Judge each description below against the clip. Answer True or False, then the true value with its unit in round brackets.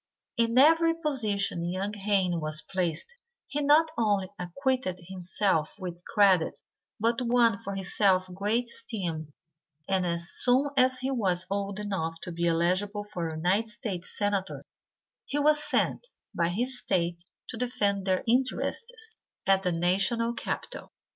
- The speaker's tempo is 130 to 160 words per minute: True (140 wpm)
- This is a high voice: True (200 Hz)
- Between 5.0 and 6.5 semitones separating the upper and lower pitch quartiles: True (5.4 semitones)